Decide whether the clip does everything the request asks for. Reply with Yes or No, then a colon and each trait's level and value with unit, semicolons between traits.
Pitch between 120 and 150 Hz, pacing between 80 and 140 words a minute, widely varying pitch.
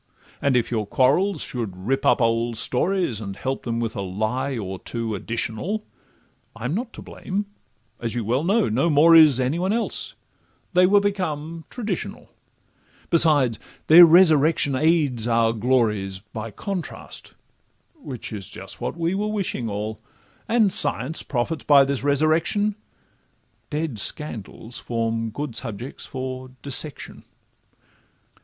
Yes: low, 135 Hz; slow, 135 wpm; wide, 6.5 semitones